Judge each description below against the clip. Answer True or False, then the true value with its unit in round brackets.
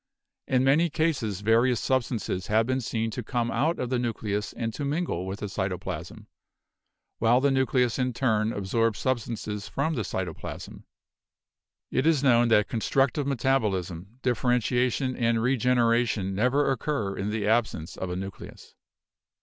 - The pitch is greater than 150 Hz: False (120 Hz)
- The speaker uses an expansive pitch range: False (3.7 semitones)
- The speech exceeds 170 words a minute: False (150 wpm)